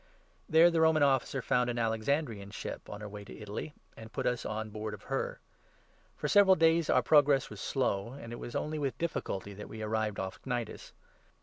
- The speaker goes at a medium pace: No, fast, 210 wpm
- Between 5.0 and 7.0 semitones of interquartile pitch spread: Yes, wide, 5.6 semitones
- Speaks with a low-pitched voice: Yes, low, 120 Hz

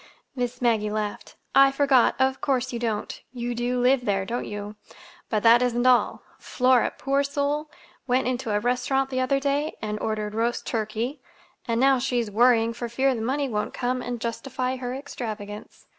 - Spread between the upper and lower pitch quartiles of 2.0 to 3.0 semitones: Yes, average, 2.7 semitones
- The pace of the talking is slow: No, average, 175 wpm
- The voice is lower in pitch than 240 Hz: No, high, 245 Hz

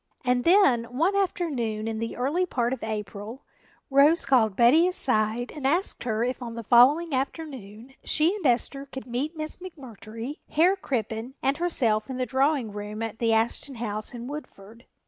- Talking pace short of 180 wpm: Yes, average, 170 wpm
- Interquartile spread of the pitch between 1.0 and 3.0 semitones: No, average, 4.9 semitones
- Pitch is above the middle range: Yes, very high, 250 Hz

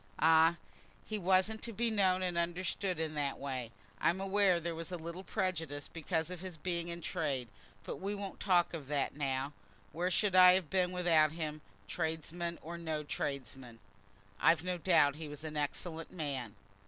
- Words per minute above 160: Yes, average, 180 wpm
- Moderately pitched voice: Yes, medium, 170 Hz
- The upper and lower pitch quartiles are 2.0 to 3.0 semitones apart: No, average, 3.4 semitones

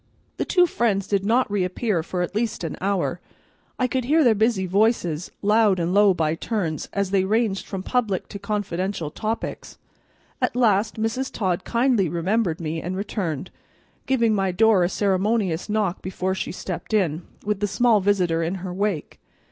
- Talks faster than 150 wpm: Yes, average, 170 wpm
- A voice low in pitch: No, high, 200 Hz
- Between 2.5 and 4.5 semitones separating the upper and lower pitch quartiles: Yes, average, 3.5 semitones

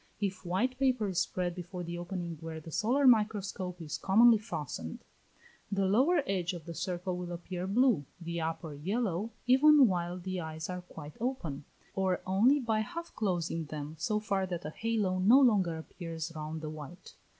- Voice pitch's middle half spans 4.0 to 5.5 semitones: Yes, average, 4.5 semitones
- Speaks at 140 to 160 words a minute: No, average, 175 wpm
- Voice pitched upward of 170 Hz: Yes, medium, 185 Hz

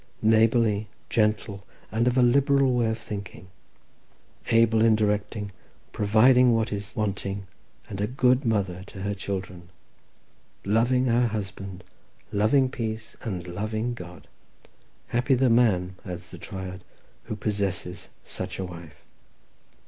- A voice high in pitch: No, low, 110 Hz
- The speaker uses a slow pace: Yes, slow, 125 wpm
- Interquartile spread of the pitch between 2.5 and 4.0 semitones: Yes, average, 3.1 semitones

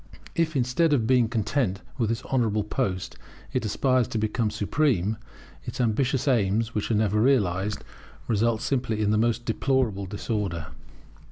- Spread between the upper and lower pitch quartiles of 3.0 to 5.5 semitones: Yes, average, 3.4 semitones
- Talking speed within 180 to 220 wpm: No, average, 150 wpm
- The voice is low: Yes, low, 110 Hz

